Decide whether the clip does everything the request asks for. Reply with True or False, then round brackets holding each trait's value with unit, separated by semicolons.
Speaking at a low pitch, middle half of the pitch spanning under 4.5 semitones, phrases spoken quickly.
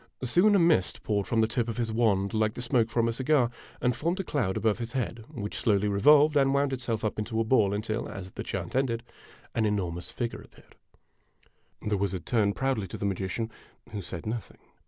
True (115 Hz; 3.5 semitones; 210 wpm)